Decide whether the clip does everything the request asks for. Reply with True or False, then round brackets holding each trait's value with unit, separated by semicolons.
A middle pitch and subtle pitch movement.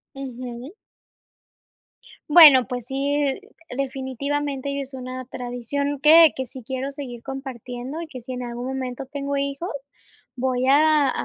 False (265 Hz; 2.0 semitones)